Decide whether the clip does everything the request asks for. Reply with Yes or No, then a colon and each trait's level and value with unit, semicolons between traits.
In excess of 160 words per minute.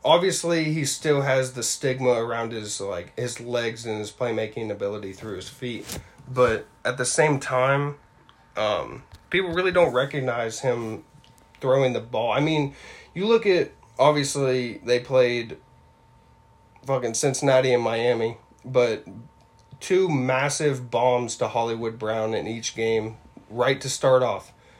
No: average, 140 wpm